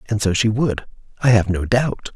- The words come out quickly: Yes, fast, 220 wpm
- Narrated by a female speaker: No, male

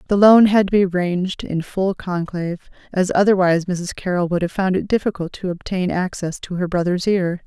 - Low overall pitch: No, medium, 185 Hz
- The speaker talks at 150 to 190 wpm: No, average, 200 wpm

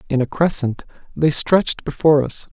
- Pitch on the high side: No, medium, 145 Hz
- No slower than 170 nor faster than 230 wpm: No, average, 160 wpm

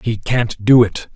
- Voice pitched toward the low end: Yes, low, 115 Hz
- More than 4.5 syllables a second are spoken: No, 3.9 syllables/s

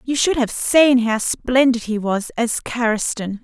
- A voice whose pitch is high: Yes, high, 240 Hz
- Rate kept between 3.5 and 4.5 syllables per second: Yes, 4.0 syllables/s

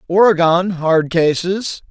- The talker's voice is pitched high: No, medium, 175 Hz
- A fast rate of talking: No, slow, 95 wpm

